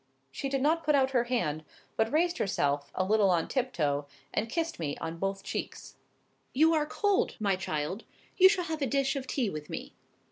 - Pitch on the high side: Yes, high, 240 Hz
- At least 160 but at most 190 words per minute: No, average, 200 wpm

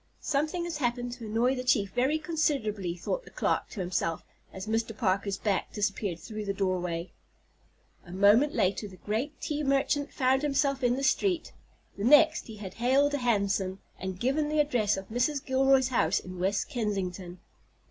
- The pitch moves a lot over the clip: Yes, wide, 6.0 semitones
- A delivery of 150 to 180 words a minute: Yes, average, 175 wpm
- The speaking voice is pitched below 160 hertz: No, high, 230 Hz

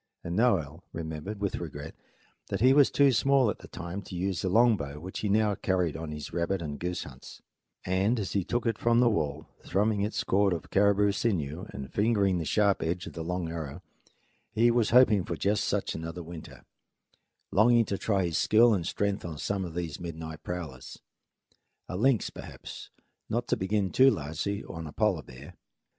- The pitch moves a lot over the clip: No, average, 4.5 semitones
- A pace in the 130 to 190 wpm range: No, average, 200 wpm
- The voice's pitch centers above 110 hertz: No, very low, 95 Hz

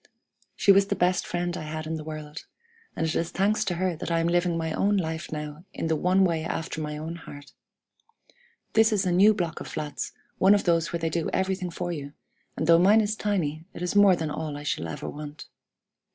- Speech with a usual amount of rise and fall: Yes, average, 3.1 semitones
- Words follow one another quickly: Yes, fast, 230 wpm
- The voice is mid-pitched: Yes, medium, 170 Hz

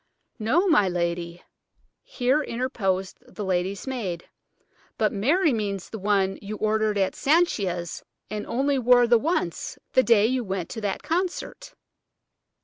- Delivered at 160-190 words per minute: No, slow, 135 wpm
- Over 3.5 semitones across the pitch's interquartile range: Yes, average, 5.3 semitones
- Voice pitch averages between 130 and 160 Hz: No, high, 215 Hz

